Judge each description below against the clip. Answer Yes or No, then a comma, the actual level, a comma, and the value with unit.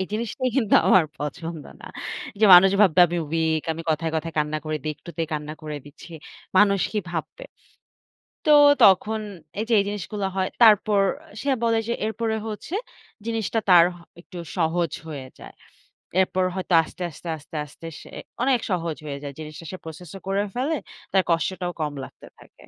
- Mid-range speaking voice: Yes, medium, 180 Hz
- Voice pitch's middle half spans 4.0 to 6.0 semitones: Yes, average, 4.7 semitones